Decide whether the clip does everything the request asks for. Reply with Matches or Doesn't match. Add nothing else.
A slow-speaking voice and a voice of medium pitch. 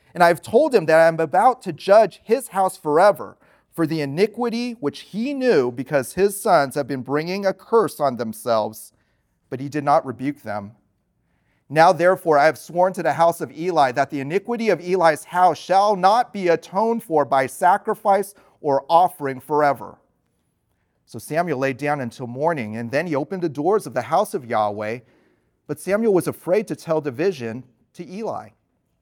Doesn't match